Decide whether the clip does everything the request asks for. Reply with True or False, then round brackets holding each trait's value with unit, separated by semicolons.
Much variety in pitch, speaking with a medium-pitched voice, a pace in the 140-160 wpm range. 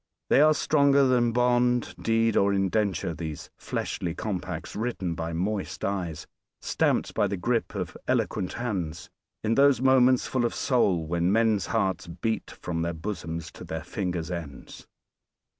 False (5.9 semitones; 100 Hz; 150 wpm)